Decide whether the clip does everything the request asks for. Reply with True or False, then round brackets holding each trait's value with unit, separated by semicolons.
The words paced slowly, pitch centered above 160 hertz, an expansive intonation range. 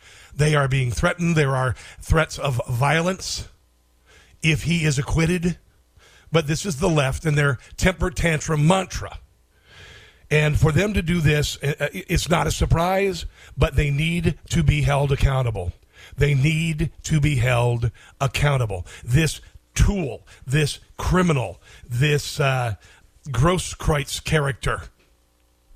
False (130 wpm; 140 Hz; 7.0 semitones)